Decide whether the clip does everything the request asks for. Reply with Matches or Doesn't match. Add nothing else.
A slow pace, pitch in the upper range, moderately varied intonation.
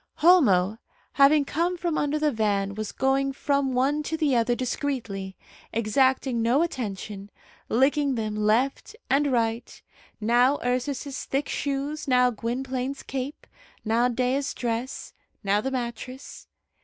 Matches